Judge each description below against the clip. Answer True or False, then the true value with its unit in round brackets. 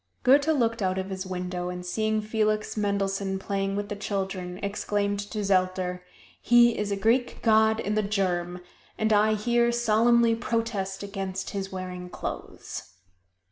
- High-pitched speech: True (200 Hz)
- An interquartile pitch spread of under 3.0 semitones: True (2.5 semitones)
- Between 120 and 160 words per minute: True (150 wpm)